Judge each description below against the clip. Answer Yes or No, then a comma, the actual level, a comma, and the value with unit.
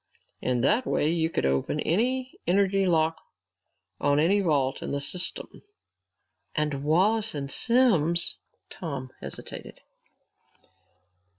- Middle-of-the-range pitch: Yes, medium, 165 Hz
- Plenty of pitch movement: Yes, wide, 5.8 semitones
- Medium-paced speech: No, slow, 115 wpm